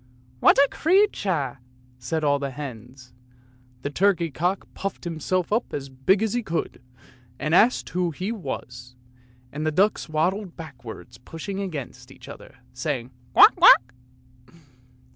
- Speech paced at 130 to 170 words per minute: Yes, average, 145 wpm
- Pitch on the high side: No, medium, 155 Hz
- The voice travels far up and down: Yes, wide, 6.3 semitones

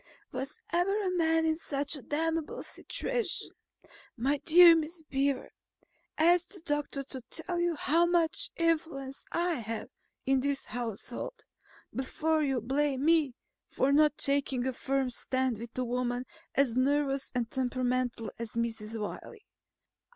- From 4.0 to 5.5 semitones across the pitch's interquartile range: Yes, average, 4.3 semitones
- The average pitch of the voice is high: Yes, very high, 280 Hz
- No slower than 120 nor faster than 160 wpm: Yes, average, 140 wpm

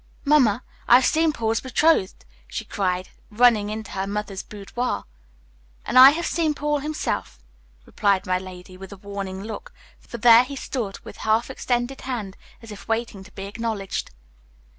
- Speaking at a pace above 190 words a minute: No, average, 160 wpm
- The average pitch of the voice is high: Yes, high, 220 Hz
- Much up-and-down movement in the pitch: No, average, 4.4 semitones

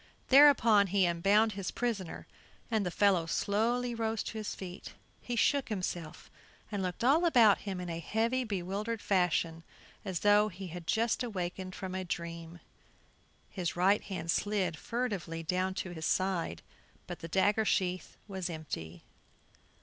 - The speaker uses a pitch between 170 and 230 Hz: Yes, high, 190 Hz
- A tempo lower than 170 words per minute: Yes, average, 150 wpm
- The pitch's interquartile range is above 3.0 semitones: Yes, average, 3.9 semitones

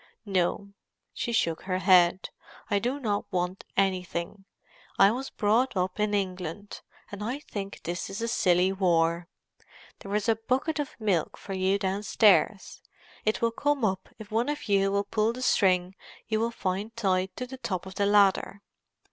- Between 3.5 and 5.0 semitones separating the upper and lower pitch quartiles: No, average, 3.1 semitones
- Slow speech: No, average, 175 wpm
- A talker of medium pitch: No, high, 200 Hz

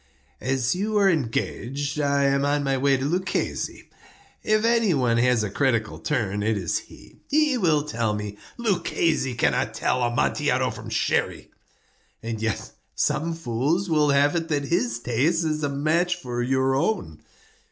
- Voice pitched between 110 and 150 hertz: Yes, medium, 140 Hz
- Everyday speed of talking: Yes, average, 160 wpm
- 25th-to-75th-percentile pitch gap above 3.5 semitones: Yes, wide, 5.5 semitones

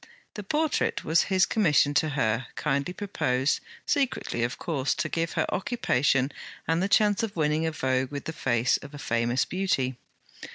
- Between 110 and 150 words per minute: No, average, 170 wpm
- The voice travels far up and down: Yes, wide, 6.2 semitones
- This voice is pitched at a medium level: Yes, medium, 150 Hz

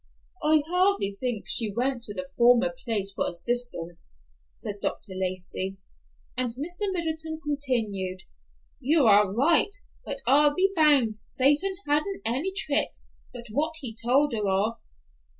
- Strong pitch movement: Yes, wide, 6.7 semitones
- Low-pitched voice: No, very high, 250 Hz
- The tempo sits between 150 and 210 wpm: No, slow, 135 wpm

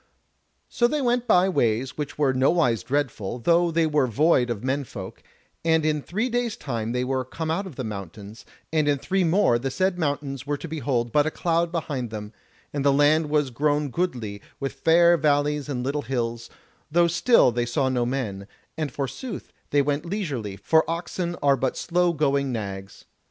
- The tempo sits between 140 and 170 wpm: No, average, 190 wpm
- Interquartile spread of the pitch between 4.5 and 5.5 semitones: Yes, average, 5.1 semitones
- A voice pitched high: No, medium, 145 Hz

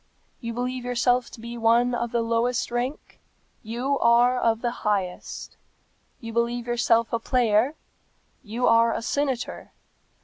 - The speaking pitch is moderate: No, high, 235 Hz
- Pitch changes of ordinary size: No, narrow, 1.3 semitones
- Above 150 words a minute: No, slow, 135 wpm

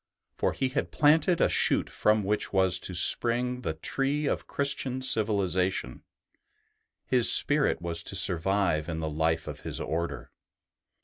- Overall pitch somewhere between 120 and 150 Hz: No, low, 100 Hz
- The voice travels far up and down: Yes, wide, 7.2 semitones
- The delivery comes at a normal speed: Yes, average, 145 wpm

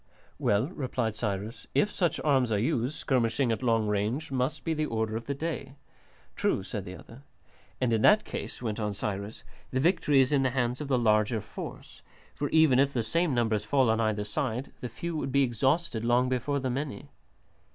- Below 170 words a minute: No, average, 200 wpm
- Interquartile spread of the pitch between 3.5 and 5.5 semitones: Yes, average, 4.0 semitones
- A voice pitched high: No, low, 125 Hz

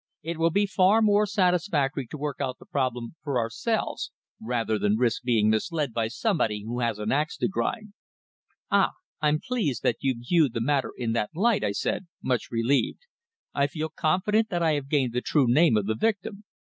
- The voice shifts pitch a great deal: Yes, wide, 7.2 semitones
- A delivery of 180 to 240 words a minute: Yes, average, 195 wpm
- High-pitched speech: No, medium, 145 Hz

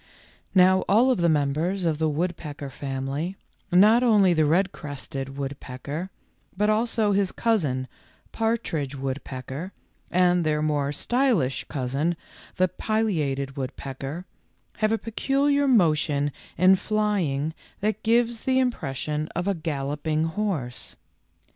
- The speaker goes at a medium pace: No, slow, 120 wpm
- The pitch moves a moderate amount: No, wide, 6.8 semitones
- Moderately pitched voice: Yes, medium, 165 Hz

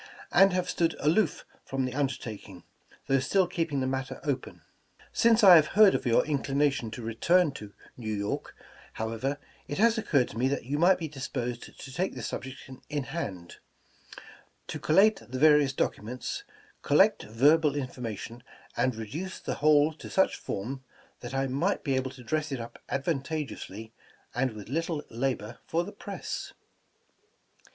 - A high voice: No, low, 135 Hz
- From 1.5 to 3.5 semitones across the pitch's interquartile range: No, average, 4.8 semitones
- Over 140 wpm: Yes, average, 160 wpm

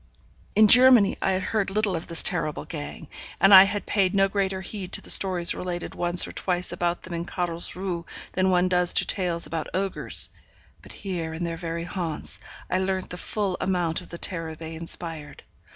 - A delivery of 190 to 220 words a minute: Yes, average, 195 wpm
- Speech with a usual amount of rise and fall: No, narrow, 2.3 semitones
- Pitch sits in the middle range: Yes, medium, 180 Hz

